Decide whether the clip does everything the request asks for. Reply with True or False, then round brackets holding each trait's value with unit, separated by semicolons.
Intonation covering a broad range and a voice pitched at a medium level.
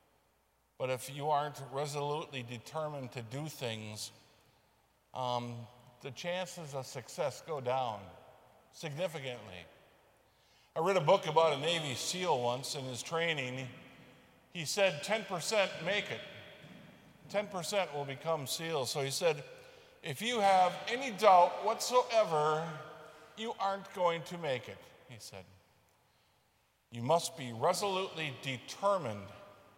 True (6.3 semitones; 155 Hz)